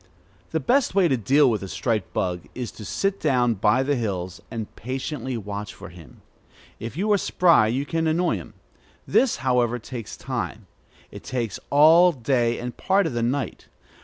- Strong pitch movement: Yes, wide, 5.8 semitones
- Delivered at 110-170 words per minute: No, average, 180 wpm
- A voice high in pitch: No, low, 125 Hz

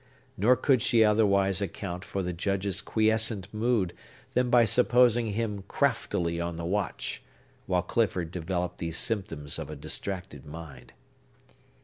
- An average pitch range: Yes, average, 4.3 semitones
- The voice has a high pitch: No, low, 100 Hz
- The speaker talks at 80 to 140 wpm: Yes, slow, 135 wpm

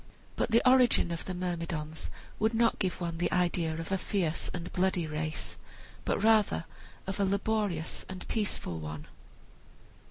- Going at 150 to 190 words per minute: Yes, average, 155 wpm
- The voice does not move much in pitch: No, average, 3.8 semitones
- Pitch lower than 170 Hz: No, medium, 180 Hz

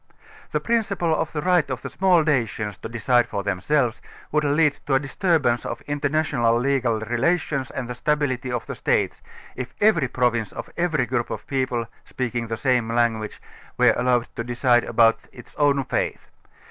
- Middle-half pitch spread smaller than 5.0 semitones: Yes, average, 4.0 semitones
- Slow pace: No, average, 175 wpm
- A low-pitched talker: Yes, low, 130 Hz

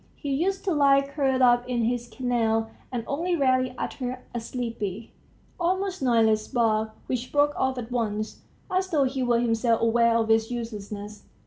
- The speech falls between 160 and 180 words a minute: Yes, average, 165 wpm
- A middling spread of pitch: Yes, average, 3.4 semitones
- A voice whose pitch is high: Yes, high, 245 Hz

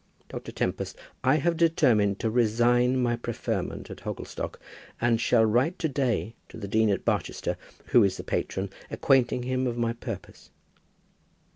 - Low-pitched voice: Yes, low, 120 Hz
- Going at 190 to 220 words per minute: No, average, 155 wpm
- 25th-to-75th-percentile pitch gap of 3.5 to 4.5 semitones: No, narrow, 2.5 semitones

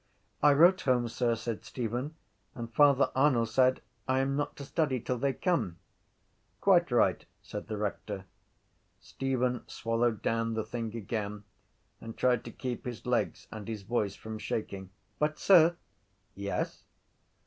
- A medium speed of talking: Yes, average, 150 wpm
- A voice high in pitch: No, low, 120 Hz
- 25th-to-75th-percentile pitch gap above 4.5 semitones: No, average, 3.4 semitones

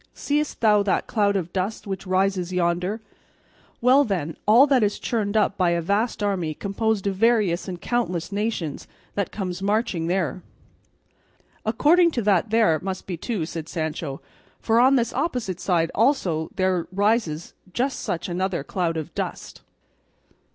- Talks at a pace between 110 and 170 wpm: Yes, average, 155 wpm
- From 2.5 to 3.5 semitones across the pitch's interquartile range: No, average, 4.3 semitones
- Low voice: No, high, 195 Hz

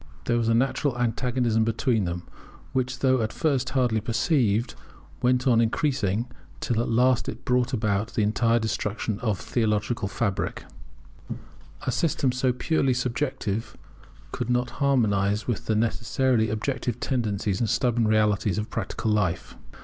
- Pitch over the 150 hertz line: No, low, 115 Hz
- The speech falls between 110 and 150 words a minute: Yes, average, 145 wpm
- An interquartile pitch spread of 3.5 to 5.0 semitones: No, average, 2.8 semitones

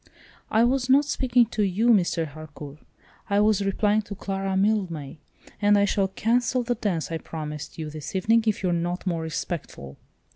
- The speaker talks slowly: No, average, 175 wpm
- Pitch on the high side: Yes, high, 195 Hz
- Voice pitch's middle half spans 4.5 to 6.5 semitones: Yes, average, 5.0 semitones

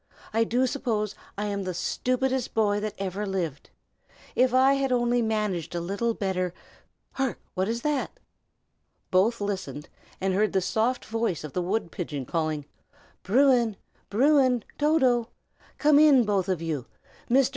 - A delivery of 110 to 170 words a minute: Yes, average, 150 wpm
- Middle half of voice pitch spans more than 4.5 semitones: Yes, average, 5.2 semitones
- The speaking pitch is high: Yes, high, 215 Hz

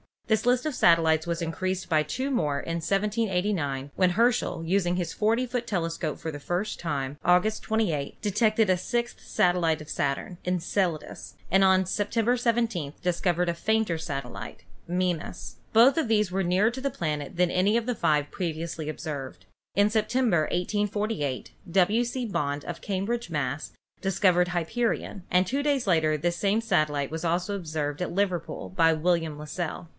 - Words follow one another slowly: No, average, 170 wpm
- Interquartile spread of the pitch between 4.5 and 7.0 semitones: Yes, average, 5.0 semitones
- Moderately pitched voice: Yes, medium, 180 Hz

